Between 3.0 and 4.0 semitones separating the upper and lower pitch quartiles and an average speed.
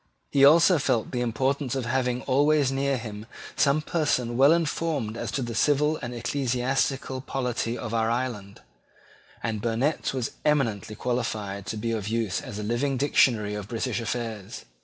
Yes: average, 3.5 semitones; average, 160 wpm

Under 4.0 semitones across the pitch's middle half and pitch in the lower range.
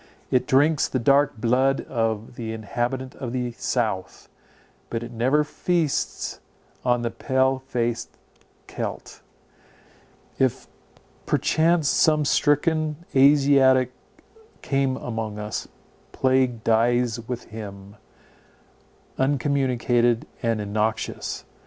Yes: average, 3.1 semitones; low, 125 Hz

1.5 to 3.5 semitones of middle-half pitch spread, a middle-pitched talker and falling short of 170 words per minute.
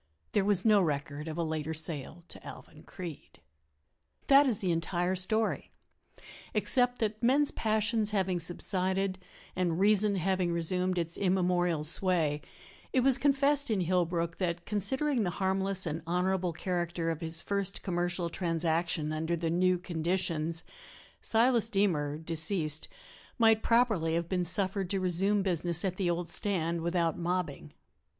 Yes: average, 3.2 semitones; medium, 180 Hz; average, 145 wpm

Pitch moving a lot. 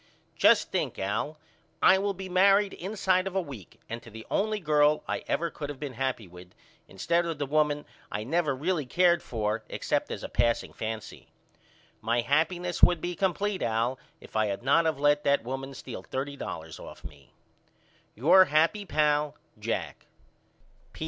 Yes: wide, 6.9 semitones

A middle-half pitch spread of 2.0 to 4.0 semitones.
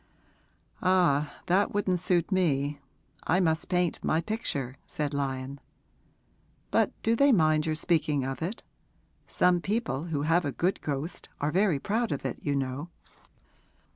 No: average, 4.4 semitones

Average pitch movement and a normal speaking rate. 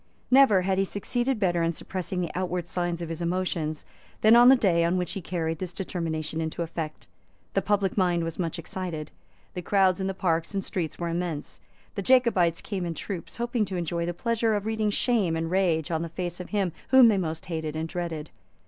No: average, 3.0 semitones; fast, 210 wpm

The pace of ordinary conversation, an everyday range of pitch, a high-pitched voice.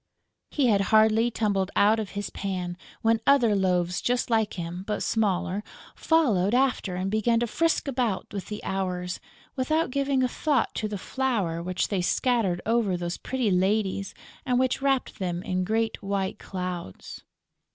Yes: average, 160 wpm; average, 4.8 semitones; high, 210 Hz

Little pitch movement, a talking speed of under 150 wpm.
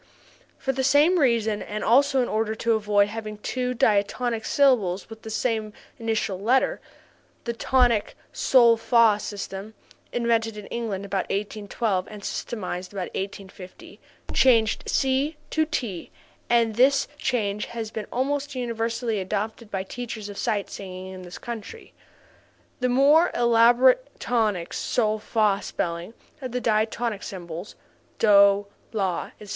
No: average, 3.2 semitones; slow, 135 wpm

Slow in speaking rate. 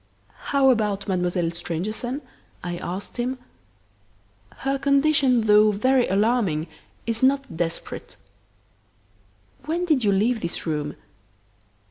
Yes: slow, 105 wpm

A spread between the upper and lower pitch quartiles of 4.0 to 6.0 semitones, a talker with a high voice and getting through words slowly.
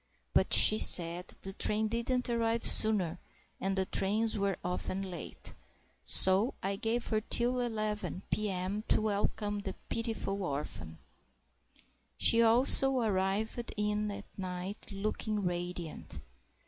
No: average, 2.9 semitones; high, 210 Hz; slow, 120 wpm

